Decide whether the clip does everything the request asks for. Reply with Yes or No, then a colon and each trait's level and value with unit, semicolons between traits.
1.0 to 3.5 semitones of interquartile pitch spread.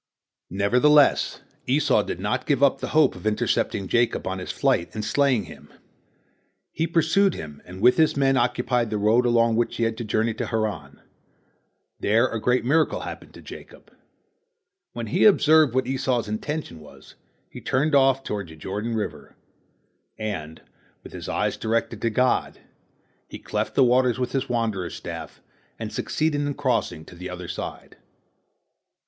No: average, 4.4 semitones